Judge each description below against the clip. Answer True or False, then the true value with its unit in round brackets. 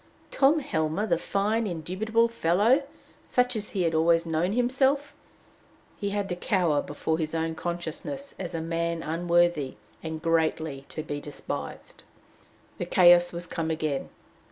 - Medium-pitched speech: True (170 Hz)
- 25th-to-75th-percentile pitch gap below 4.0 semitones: False (4.4 semitones)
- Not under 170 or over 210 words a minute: False (140 wpm)